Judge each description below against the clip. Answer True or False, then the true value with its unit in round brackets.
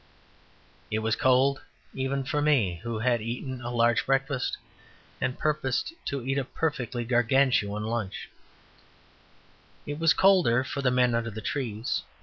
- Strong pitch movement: False (2.9 semitones)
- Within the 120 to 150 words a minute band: True (140 wpm)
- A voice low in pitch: True (125 Hz)